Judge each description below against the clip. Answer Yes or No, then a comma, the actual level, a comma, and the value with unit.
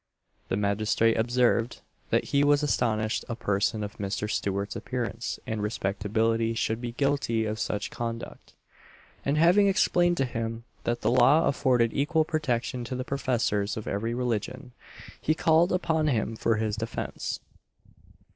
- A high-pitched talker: No, low, 115 Hz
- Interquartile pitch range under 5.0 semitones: Yes, average, 4.1 semitones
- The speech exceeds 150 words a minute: No, average, 145 wpm